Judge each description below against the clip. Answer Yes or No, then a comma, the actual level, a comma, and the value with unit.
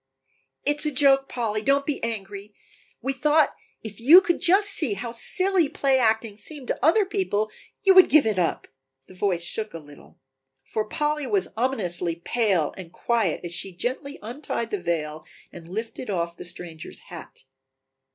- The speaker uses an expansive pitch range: Yes, wide, 7.6 semitones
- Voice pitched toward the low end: No, high, 225 Hz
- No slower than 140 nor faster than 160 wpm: No, average, 170 wpm